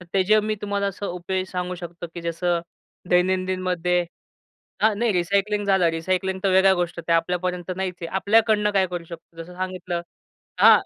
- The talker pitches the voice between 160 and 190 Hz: Yes, medium, 185 Hz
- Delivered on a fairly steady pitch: Yes, narrow, 1.9 semitones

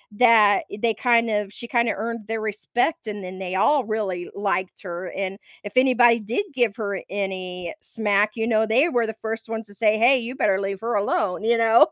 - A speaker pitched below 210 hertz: No, high, 220 Hz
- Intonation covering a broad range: No, average, 2.8 semitones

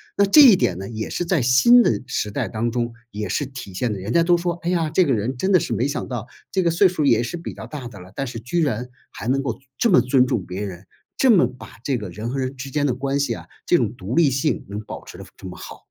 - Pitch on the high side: No, low, 130 Hz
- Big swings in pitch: Yes, wide, 6.8 semitones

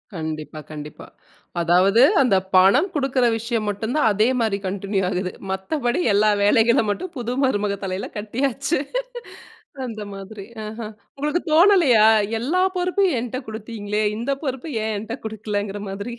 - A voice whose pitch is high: Yes, high, 220 Hz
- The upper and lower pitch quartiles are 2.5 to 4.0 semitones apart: No, average, 4.4 semitones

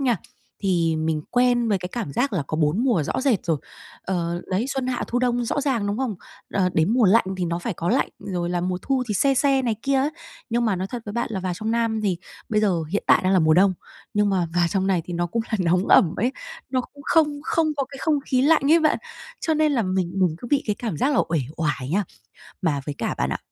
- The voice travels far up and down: Yes, wide, 6.2 semitones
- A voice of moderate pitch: No, high, 210 Hz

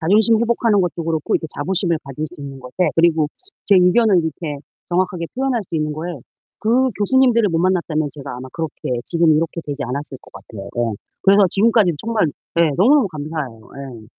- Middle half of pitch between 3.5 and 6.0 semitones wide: Yes, wide, 5.6 semitones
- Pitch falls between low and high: Yes, medium, 165 Hz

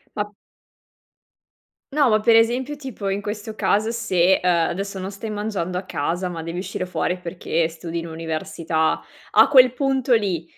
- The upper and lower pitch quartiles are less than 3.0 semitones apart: No, average, 5.0 semitones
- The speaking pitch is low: No, high, 195 Hz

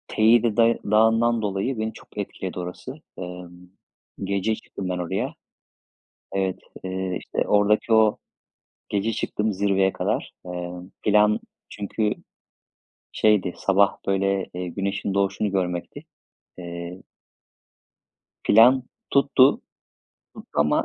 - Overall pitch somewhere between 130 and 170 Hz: No, low, 100 Hz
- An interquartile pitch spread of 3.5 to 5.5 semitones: No, average, 3.1 semitones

